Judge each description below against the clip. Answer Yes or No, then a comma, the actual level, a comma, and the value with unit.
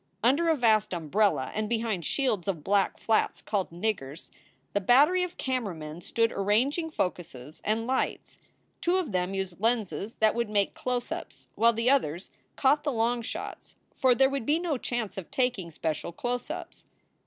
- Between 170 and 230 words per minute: Yes, average, 175 wpm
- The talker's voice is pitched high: Yes, high, 225 Hz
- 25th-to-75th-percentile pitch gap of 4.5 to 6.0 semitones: Yes, average, 5.1 semitones